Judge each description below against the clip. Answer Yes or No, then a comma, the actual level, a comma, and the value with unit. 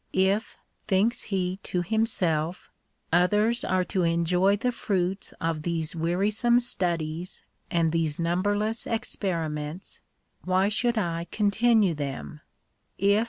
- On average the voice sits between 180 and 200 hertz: Yes, medium, 185 Hz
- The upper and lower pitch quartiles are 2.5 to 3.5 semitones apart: No, average, 3.9 semitones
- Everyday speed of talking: No, slow, 120 wpm